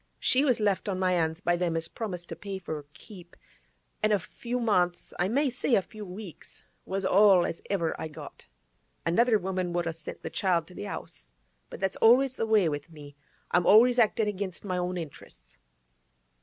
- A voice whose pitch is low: No, medium, 185 Hz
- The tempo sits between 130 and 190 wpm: No, average, 200 wpm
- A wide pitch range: No, average, 3.7 semitones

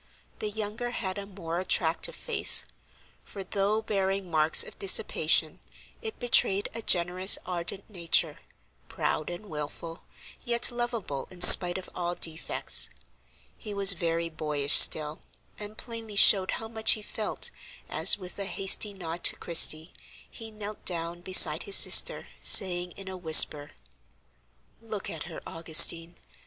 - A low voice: No, medium, 185 Hz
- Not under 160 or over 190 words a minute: No, average, 140 wpm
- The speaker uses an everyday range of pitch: Yes, average, 3.9 semitones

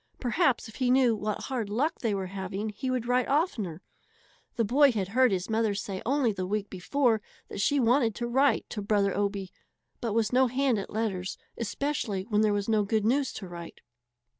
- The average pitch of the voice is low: No, high, 220 Hz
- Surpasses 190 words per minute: Yes, average, 200 wpm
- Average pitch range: Yes, average, 4.2 semitones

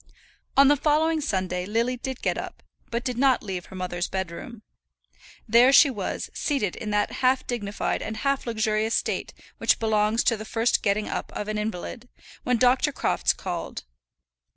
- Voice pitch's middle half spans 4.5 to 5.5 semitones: No, average, 3.6 semitones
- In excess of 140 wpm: Yes, average, 170 wpm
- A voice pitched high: Yes, high, 225 Hz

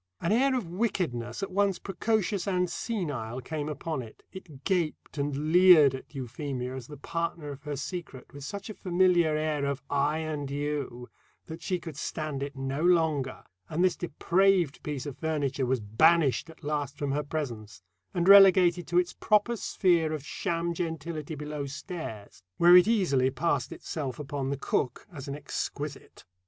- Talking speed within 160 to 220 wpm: Yes, average, 170 wpm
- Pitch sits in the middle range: Yes, medium, 155 Hz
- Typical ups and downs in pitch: Yes, average, 4.1 semitones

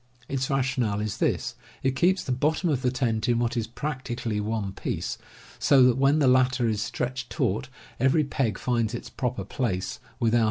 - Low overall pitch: Yes, low, 125 Hz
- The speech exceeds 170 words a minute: Yes, average, 185 wpm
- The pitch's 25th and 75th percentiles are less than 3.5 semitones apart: Yes, average, 2.8 semitones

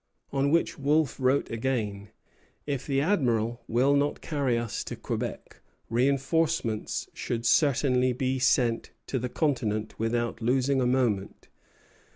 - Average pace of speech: No, slow, 130 wpm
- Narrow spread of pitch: No, average, 3.1 semitones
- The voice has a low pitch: Yes, low, 130 Hz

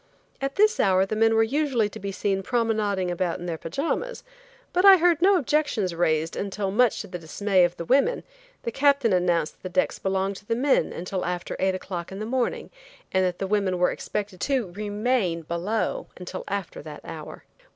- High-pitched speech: Yes, high, 205 Hz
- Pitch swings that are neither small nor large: No, wide, 6.1 semitones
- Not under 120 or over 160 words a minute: No, average, 200 wpm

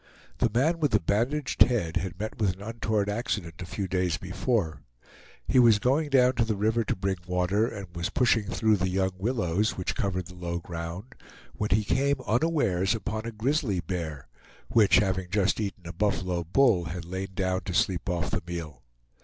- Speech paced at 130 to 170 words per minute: No, average, 190 wpm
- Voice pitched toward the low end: Yes, low, 100 Hz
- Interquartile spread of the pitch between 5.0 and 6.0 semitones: No, average, 4.1 semitones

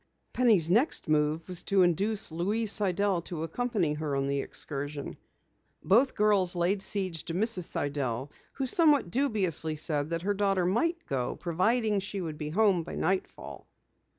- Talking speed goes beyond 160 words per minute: No, average, 155 wpm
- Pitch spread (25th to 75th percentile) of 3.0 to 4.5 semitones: No, average, 5.0 semitones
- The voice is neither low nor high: Yes, medium, 180 Hz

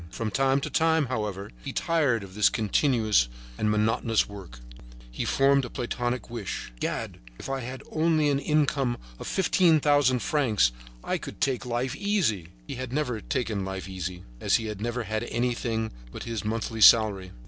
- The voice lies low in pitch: Yes, low, 120 Hz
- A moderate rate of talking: Yes, average, 170 wpm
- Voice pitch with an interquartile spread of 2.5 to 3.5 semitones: No, average, 4.3 semitones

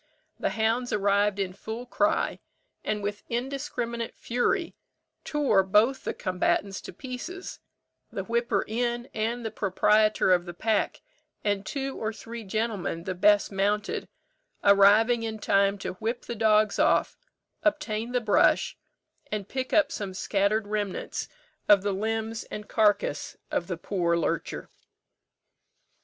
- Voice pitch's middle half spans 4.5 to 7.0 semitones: No, average, 2.9 semitones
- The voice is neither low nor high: No, high, 215 Hz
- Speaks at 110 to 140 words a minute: Yes, slow, 135 wpm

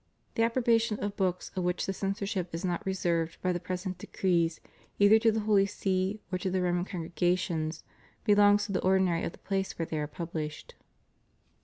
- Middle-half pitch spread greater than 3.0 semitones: No, average, 2.7 semitones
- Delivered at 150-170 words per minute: No, average, 190 wpm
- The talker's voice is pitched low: No, medium, 185 Hz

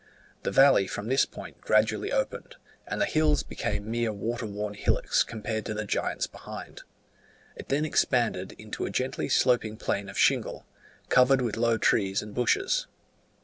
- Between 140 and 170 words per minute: Yes, average, 160 wpm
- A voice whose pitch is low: Yes, low, 115 Hz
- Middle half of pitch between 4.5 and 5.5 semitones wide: No, average, 4.1 semitones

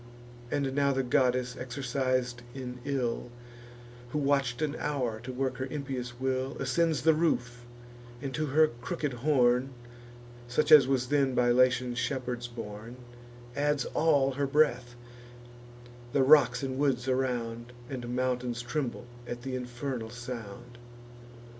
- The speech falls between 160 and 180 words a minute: No, slow, 135 wpm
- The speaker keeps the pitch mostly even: Yes, narrow, 2.2 semitones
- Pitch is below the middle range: Yes, low, 130 Hz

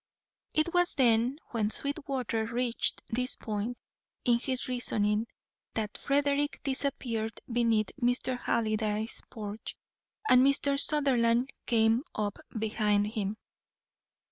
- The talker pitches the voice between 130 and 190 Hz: No, high, 235 Hz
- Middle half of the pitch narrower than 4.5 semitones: Yes, average, 3.4 semitones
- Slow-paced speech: Yes, slow, 100 wpm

